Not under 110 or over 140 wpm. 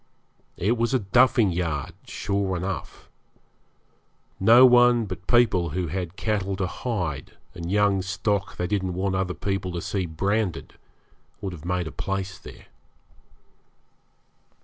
Yes: slow, 135 wpm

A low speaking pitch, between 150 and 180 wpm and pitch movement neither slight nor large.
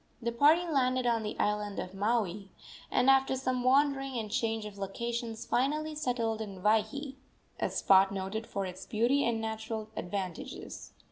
No: high, 225 Hz; average, 155 wpm; average, 3.7 semitones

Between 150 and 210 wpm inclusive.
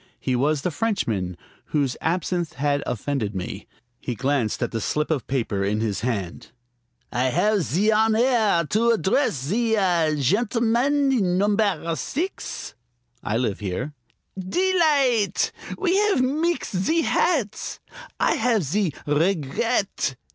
No: slow, 135 wpm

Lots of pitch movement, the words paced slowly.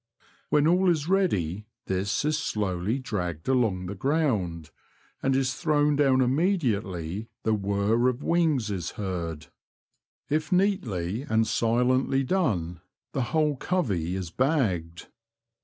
Yes: wide, 8.0 semitones; slow, 125 wpm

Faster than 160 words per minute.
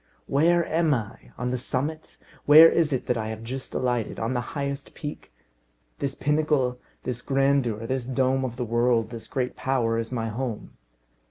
Yes: average, 175 wpm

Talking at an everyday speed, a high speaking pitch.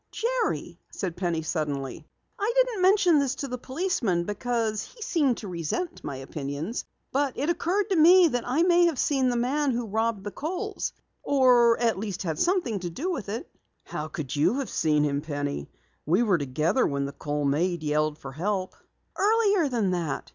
Yes: average, 185 wpm; high, 230 Hz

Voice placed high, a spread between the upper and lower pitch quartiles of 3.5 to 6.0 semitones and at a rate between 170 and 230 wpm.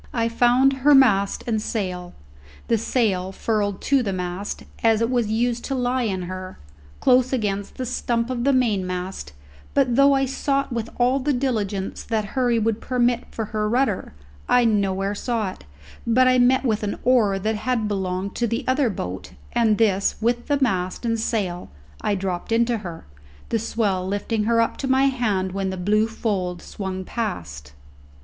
Yes: high, 225 Hz; average, 4.1 semitones; average, 180 wpm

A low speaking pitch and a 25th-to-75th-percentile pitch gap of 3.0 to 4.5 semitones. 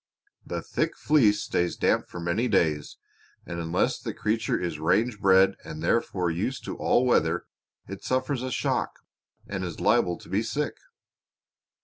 No: very low, 95 Hz; wide, 5.4 semitones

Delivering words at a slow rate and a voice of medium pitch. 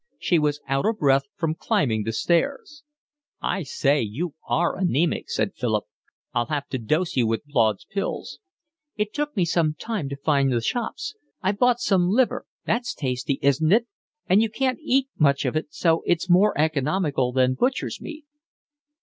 No: average, 175 wpm; medium, 155 Hz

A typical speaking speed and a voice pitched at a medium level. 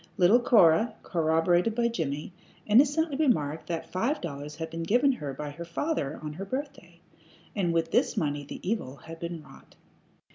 Yes: average, 170 wpm; medium, 170 Hz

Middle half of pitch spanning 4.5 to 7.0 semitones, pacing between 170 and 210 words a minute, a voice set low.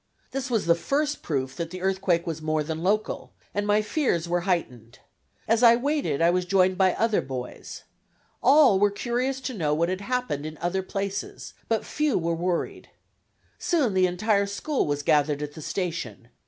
No: wide, 5.6 semitones; average, 180 wpm; medium, 185 Hz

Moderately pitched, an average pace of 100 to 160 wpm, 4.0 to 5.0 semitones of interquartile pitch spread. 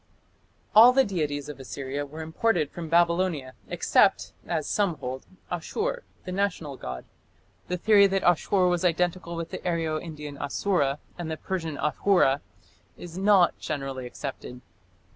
Yes: medium, 165 Hz; average, 140 wpm; average, 4.3 semitones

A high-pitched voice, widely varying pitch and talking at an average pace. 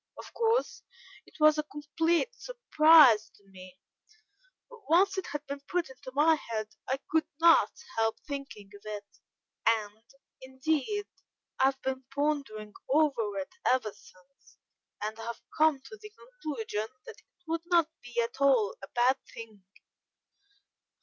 Yes: very high, 270 Hz; wide, 6.2 semitones; average, 145 wpm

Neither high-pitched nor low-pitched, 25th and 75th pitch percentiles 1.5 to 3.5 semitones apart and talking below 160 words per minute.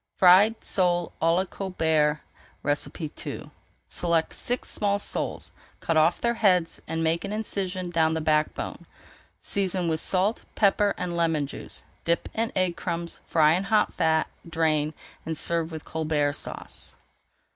Yes: medium, 170 Hz; average, 3.1 semitones; average, 150 wpm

